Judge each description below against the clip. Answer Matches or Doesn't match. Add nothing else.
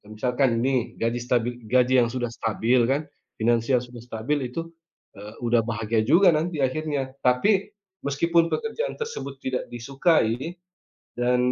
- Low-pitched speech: Matches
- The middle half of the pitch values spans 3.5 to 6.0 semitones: Matches